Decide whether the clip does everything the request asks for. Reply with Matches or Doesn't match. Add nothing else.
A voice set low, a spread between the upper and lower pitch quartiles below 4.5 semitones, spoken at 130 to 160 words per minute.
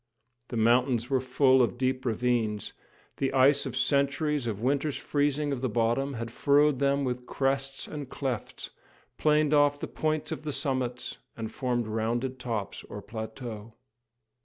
Matches